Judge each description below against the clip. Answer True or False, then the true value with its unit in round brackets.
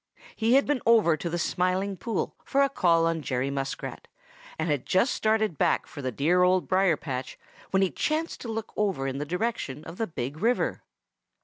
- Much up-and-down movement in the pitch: True (6.9 semitones)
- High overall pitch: False (180 Hz)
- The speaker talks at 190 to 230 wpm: True (200 wpm)